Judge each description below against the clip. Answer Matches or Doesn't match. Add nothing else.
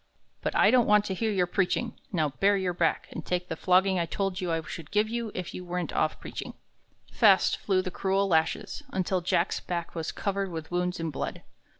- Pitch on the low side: Doesn't match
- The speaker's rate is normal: Doesn't match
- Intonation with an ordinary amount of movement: Doesn't match